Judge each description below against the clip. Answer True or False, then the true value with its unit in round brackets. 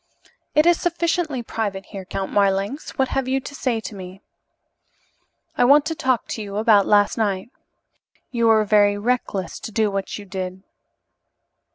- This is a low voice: False (215 Hz)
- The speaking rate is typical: True (155 wpm)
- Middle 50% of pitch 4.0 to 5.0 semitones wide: True (4.7 semitones)